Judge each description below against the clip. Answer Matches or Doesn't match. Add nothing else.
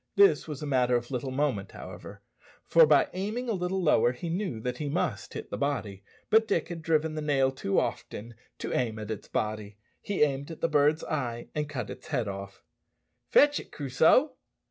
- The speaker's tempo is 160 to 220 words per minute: Matches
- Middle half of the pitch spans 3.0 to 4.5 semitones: Doesn't match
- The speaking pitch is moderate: Matches